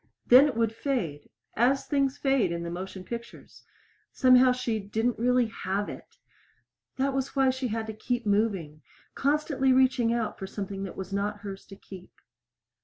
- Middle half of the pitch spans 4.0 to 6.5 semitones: Yes, average, 4.8 semitones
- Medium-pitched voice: No, high, 230 Hz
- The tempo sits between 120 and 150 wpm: No, average, 170 wpm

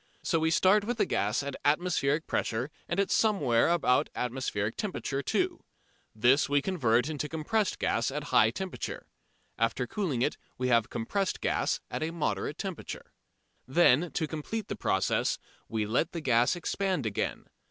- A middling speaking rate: Yes, average, 165 wpm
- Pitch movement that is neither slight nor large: No, wide, 6.3 semitones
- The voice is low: No, medium, 145 Hz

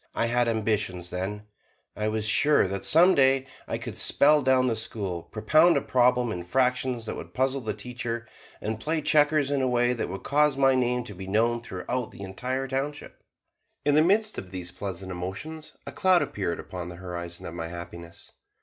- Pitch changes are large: Yes, wide, 5.9 semitones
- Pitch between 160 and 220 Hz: No, low, 120 Hz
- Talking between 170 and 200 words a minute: Yes, average, 195 wpm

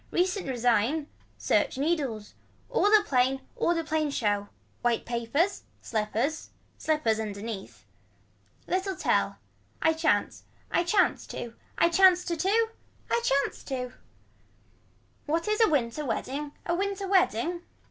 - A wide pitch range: Yes, wide, 7.1 semitones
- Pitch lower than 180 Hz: No, very high, 305 Hz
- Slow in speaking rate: Yes, slow, 125 wpm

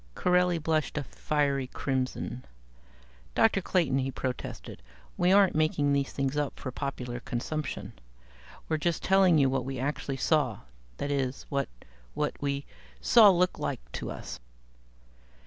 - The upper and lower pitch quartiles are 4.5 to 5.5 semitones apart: No, average, 3.5 semitones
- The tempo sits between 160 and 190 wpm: No, average, 140 wpm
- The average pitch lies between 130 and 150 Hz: Yes, medium, 140 Hz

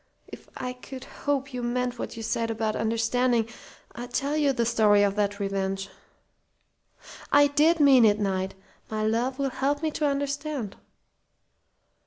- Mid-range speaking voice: No, high, 245 Hz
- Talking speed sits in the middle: Yes, average, 155 wpm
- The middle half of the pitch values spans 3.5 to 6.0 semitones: Yes, average, 4.4 semitones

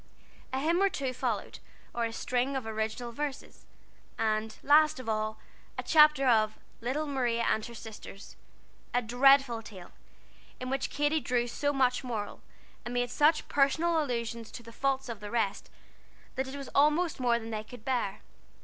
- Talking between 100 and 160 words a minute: No, average, 170 wpm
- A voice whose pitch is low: No, high, 245 Hz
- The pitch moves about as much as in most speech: Yes, average, 3.6 semitones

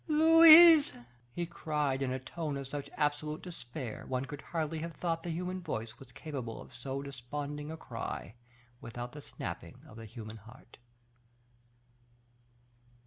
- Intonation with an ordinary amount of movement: Yes, average, 5.0 semitones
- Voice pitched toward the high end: No, medium, 145 Hz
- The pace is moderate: Yes, average, 145 wpm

